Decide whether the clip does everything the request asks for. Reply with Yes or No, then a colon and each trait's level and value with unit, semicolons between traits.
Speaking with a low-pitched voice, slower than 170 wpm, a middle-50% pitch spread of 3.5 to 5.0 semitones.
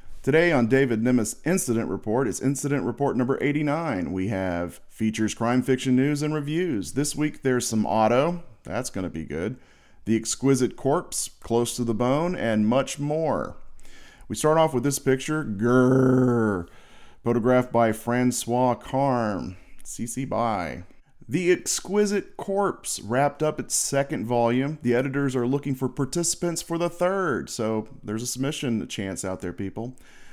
Yes: low, 125 Hz; average, 150 wpm; average, 4.0 semitones